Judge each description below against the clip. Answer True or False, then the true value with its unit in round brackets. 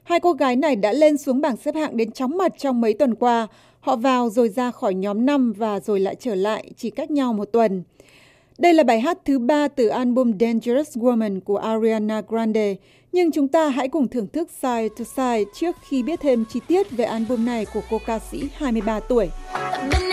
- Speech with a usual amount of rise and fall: True (4.6 semitones)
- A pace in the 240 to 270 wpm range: False (215 wpm)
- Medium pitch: False (245 Hz)